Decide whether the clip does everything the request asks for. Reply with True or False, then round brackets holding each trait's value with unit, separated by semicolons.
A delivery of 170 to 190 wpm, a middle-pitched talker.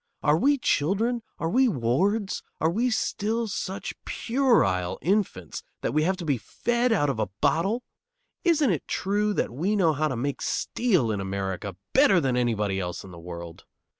True (175 wpm; 165 Hz)